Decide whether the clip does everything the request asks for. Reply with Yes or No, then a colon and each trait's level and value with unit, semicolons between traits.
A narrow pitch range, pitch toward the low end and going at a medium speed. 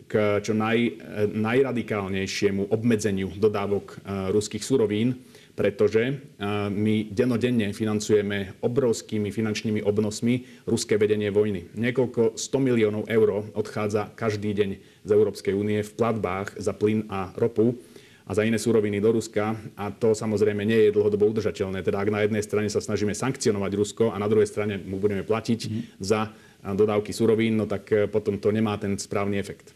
Yes: narrow, 1.6 semitones; low, 105 Hz; average, 150 wpm